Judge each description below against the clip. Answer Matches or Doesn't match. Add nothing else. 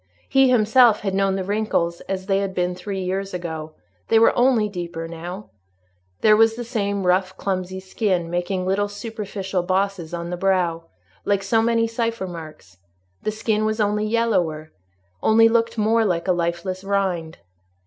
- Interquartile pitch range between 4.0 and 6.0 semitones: Doesn't match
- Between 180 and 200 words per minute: Doesn't match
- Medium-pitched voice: Doesn't match